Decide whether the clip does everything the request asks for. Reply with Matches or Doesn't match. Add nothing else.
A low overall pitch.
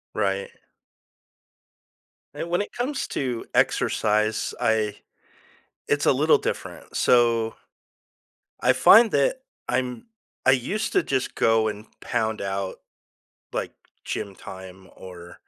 Matches